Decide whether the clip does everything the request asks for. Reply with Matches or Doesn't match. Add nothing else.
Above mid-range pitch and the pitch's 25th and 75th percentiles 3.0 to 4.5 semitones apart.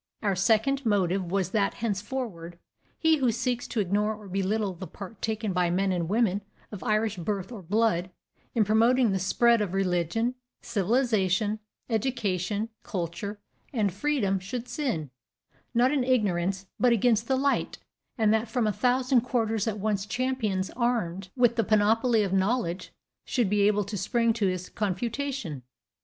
Matches